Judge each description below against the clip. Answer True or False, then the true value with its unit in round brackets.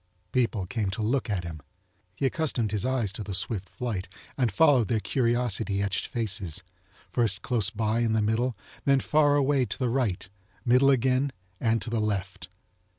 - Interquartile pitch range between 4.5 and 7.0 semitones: False (3.8 semitones)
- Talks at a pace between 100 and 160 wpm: False (175 wpm)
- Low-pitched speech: True (115 Hz)